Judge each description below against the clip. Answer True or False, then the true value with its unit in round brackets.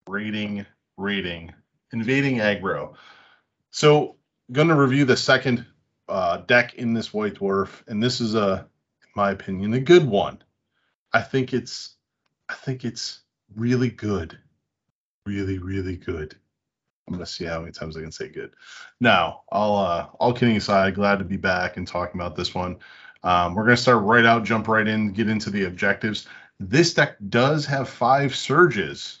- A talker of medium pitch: False (105 Hz)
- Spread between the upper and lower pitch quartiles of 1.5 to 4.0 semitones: False (4.4 semitones)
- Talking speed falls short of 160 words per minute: False (165 wpm)